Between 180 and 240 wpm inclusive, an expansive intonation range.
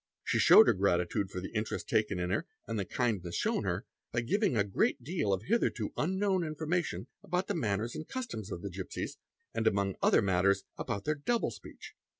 Yes: average, 195 wpm; wide, 8.7 semitones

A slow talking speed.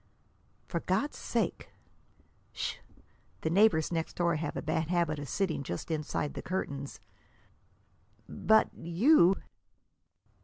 Yes: slow, 115 wpm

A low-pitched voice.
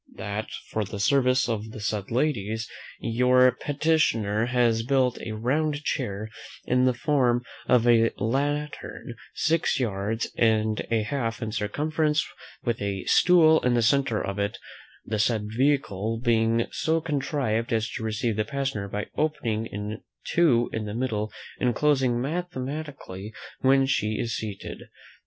Yes: low, 120 Hz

